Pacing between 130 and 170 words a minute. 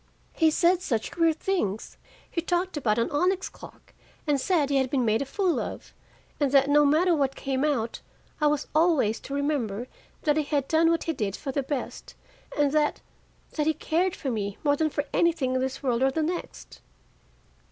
No: average, 200 wpm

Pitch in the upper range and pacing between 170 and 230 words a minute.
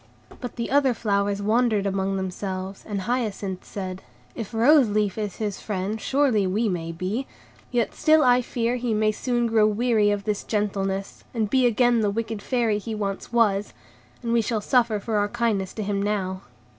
Yes: high, 215 Hz; average, 180 wpm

